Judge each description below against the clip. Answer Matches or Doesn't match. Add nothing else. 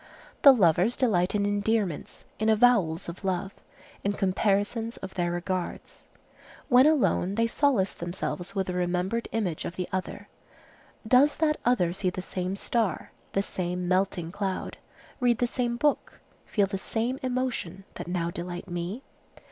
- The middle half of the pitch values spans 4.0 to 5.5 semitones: Matches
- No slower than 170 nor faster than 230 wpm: Doesn't match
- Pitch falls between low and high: Doesn't match